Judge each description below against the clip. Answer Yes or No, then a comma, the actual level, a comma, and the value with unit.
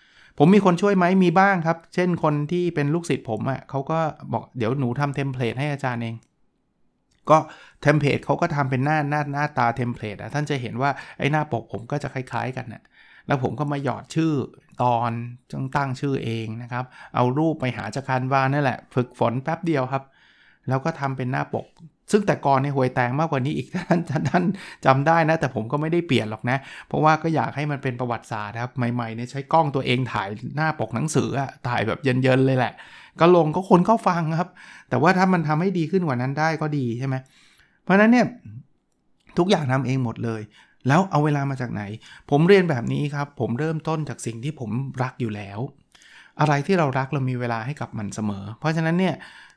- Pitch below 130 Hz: No, medium, 140 Hz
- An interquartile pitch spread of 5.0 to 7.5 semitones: No, average, 4.2 semitones